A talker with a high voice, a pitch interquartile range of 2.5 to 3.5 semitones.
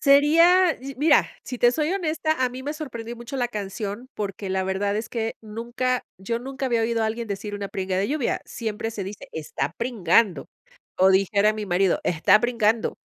No: high, 225 Hz; average, 4.3 semitones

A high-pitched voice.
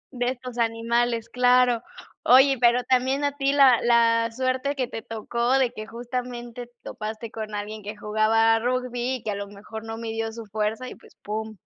Yes: high, 235 Hz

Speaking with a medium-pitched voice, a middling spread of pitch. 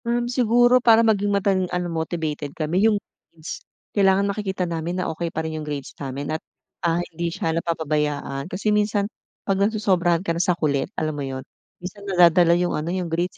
Yes: medium, 175 Hz; average, 3.9 semitones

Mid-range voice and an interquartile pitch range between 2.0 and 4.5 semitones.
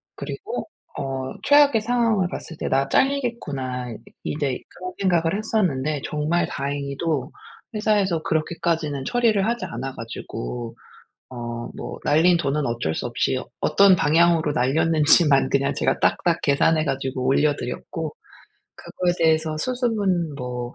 No: medium, 155 Hz; average, 5.3 semitones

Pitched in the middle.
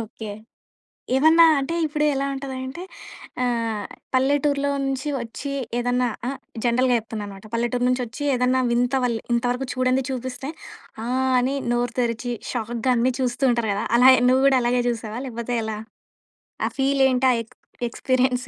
No: very high, 250 Hz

